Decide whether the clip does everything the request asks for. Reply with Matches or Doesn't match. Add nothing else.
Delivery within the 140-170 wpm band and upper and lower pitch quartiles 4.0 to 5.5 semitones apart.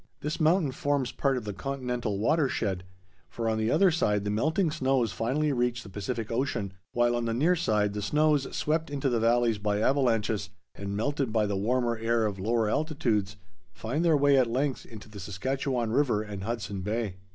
Doesn't match